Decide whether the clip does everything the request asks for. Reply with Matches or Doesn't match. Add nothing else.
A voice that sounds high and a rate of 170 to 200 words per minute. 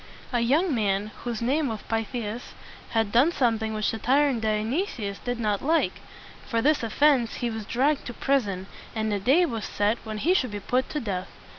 Matches